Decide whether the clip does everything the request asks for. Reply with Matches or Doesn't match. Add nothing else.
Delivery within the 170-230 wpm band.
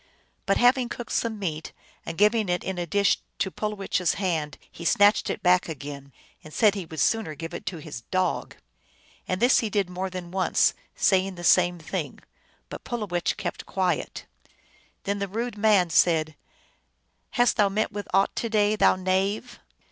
Matches